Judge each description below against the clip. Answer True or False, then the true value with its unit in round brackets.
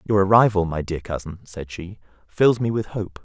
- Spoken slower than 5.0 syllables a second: False (5.1 syllables/s)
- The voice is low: True (95 Hz)